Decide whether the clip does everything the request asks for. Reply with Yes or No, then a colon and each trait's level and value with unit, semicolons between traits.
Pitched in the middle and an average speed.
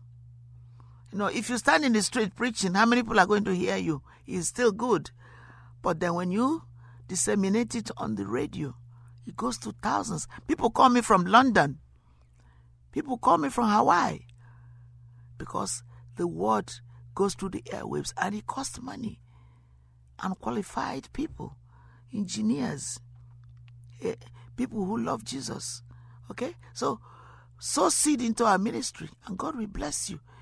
No: low, 120 Hz; average, 145 wpm